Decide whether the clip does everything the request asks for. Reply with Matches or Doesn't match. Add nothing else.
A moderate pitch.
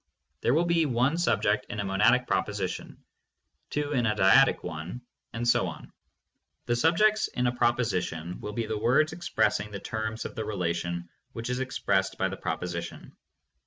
Doesn't match